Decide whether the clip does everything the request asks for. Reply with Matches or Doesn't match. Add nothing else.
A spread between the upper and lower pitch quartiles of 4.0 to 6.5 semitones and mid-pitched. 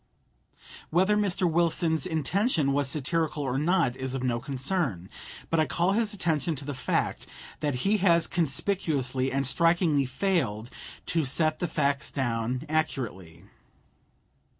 Matches